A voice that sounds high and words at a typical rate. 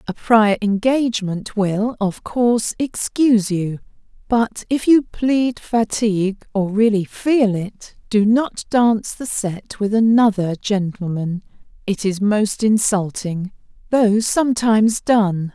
No: high, 215 Hz; slow, 125 wpm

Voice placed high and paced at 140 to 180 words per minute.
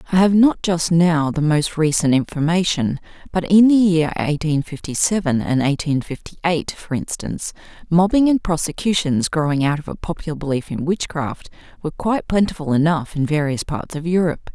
No: medium, 165 Hz; average, 175 wpm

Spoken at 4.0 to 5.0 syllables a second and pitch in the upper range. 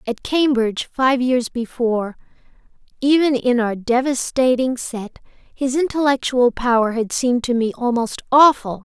Yes: 4.6 syllables/s; very high, 250 Hz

